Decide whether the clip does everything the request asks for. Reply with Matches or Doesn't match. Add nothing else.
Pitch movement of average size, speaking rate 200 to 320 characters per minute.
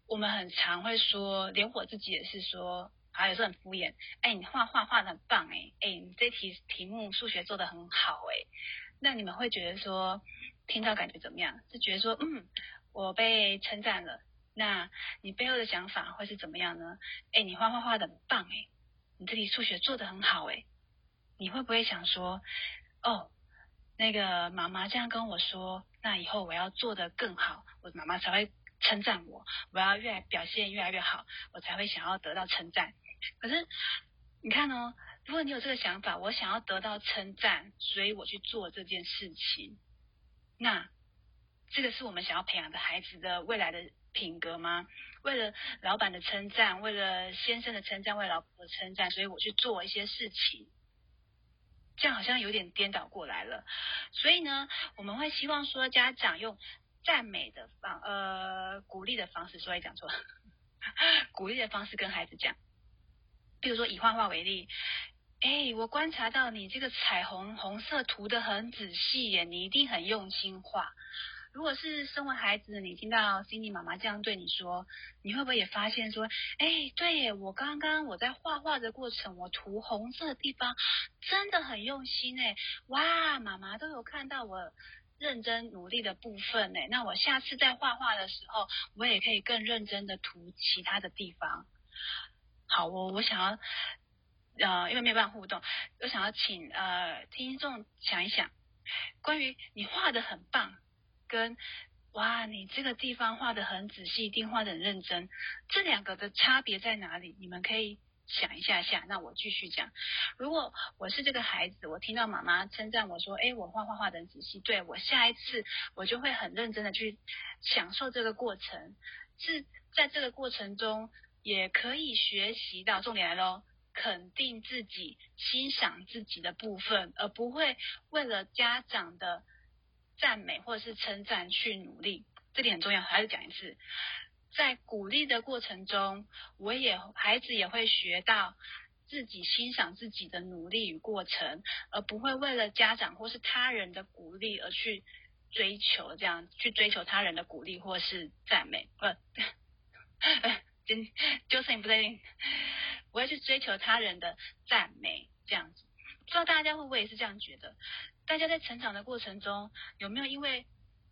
Matches